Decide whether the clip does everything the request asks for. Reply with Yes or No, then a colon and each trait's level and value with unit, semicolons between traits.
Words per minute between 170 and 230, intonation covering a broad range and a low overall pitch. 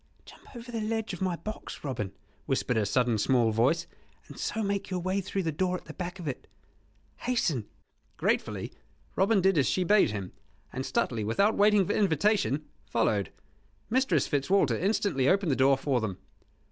No: average, 175 wpm; wide, 7.7 semitones; medium, 175 Hz